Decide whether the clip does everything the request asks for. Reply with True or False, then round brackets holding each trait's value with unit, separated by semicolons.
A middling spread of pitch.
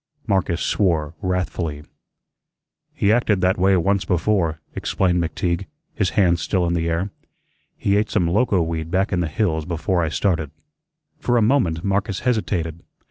True (3.1 semitones)